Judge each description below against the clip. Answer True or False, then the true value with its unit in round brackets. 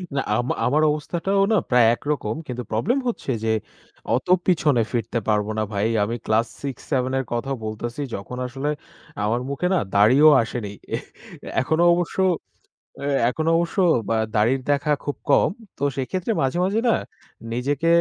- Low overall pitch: True (130 Hz)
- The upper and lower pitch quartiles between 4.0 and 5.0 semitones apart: True (4.7 semitones)